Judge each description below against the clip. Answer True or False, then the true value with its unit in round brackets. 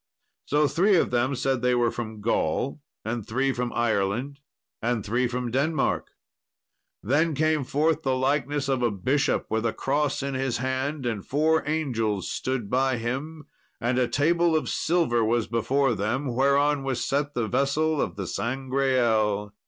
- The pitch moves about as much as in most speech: True (3.5 semitones)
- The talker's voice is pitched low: True (130 Hz)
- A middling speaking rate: True (160 wpm)